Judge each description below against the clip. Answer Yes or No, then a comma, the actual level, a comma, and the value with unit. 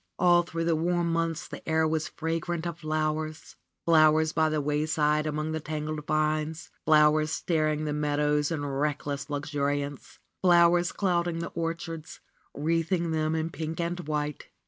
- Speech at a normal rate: Yes, average, 150 wpm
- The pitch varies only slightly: Yes, narrow, 1.6 semitones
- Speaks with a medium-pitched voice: Yes, medium, 155 Hz